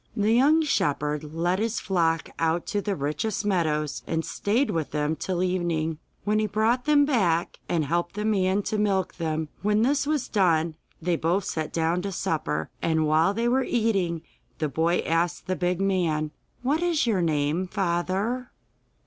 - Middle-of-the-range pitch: Yes, medium, 180 Hz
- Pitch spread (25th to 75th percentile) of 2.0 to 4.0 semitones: No, average, 4.8 semitones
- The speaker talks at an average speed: Yes, average, 175 wpm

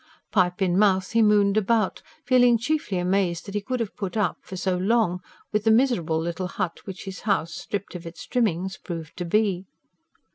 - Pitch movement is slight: No, average, 3.3 semitones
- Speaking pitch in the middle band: No, high, 195 Hz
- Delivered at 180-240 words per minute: Yes, average, 190 wpm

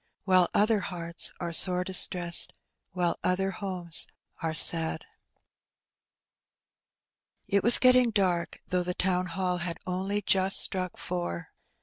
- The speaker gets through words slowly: Yes, slow, 125 wpm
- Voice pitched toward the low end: No, medium, 180 Hz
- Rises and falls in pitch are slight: Yes, narrow, 2.0 semitones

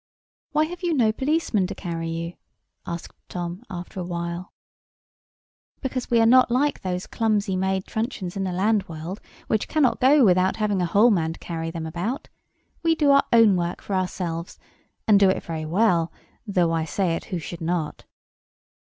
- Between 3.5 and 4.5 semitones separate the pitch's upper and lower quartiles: No, average, 4.9 semitones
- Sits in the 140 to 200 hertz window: Yes, high, 190 Hz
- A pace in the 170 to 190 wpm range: Yes, average, 180 wpm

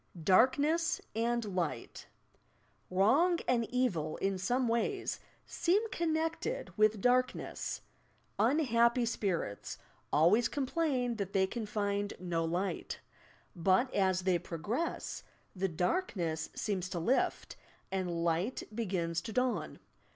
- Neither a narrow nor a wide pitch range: No, wide, 5.7 semitones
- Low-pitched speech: No, high, 215 Hz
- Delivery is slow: Yes, slow, 110 wpm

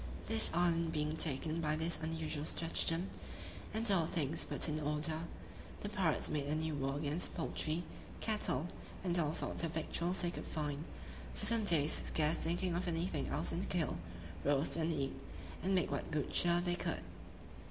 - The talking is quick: No, average, 180 wpm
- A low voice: No, medium, 165 Hz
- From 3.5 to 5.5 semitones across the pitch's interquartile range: No, narrow, 2.4 semitones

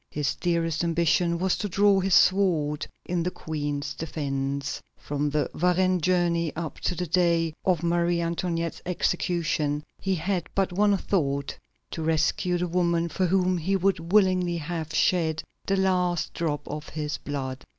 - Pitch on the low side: No, medium, 170 Hz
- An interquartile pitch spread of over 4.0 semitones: No, average, 2.7 semitones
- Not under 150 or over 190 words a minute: Yes, average, 155 wpm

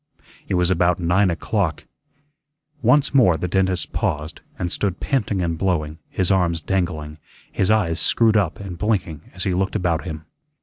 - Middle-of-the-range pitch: No, very low, 90 Hz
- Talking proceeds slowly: No, average, 165 wpm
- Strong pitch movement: No, average, 2.8 semitones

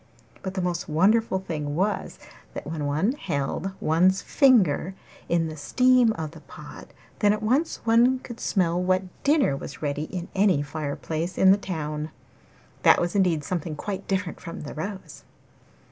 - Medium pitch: Yes, medium, 180 Hz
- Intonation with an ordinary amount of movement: Yes, average, 4.6 semitones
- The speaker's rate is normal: Yes, average, 165 wpm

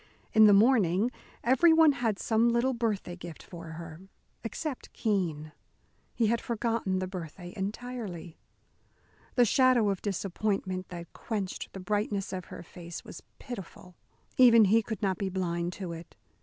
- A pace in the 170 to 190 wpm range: No, average, 145 wpm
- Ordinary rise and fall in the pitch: Yes, average, 4.6 semitones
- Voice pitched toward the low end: No, high, 200 Hz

